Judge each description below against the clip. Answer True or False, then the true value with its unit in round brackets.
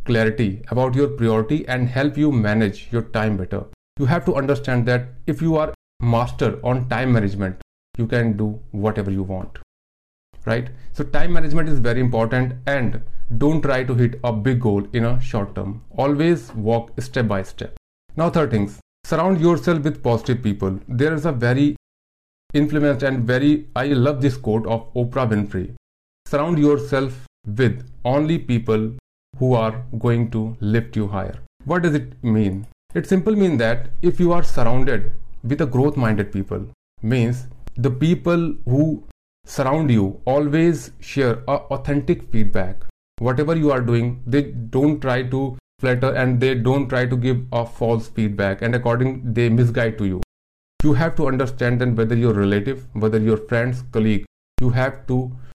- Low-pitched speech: True (125 Hz)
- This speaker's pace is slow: False (165 wpm)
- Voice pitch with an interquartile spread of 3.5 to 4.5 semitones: True (4.0 semitones)